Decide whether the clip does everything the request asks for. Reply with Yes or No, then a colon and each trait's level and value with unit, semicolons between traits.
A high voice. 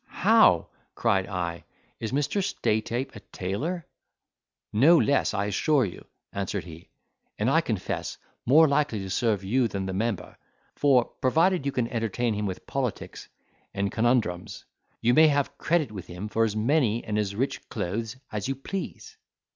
No: low, 115 Hz